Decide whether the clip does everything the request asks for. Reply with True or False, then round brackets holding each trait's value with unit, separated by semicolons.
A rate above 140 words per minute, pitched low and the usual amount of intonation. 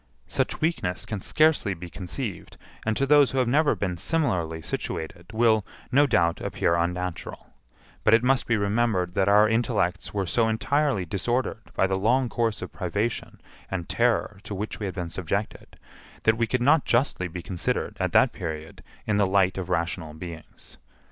True (175 wpm; 100 Hz; 5.0 semitones)